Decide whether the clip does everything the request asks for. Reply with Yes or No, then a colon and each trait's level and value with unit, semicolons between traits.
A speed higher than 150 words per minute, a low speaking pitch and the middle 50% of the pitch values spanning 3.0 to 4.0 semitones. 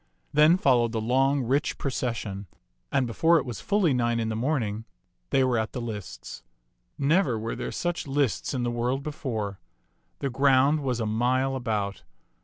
Yes: average, 175 wpm; low, 125 Hz; average, 3.5 semitones